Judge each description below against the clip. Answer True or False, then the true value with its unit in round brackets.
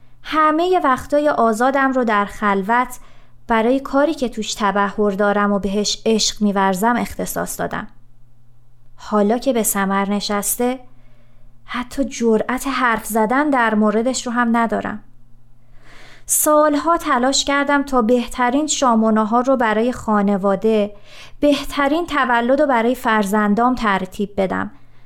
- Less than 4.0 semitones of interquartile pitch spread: False (4.3 semitones)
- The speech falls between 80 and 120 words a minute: True (115 wpm)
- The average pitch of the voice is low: False (225 Hz)